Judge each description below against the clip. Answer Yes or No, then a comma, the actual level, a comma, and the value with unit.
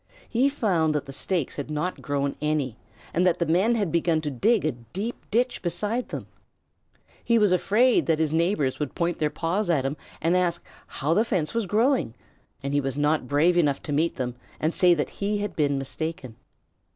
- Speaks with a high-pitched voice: No, medium, 165 Hz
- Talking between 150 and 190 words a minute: No, average, 200 wpm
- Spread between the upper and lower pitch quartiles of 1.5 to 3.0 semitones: No, wide, 5.4 semitones